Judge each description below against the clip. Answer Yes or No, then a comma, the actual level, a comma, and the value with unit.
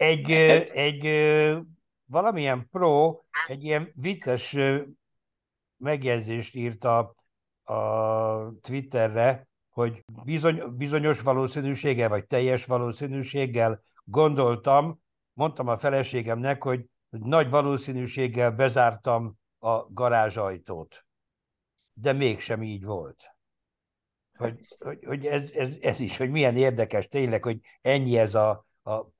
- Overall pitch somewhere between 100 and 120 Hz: No, low, 130 Hz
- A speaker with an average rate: No, slow, 95 wpm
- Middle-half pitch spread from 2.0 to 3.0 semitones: No, average, 3.8 semitones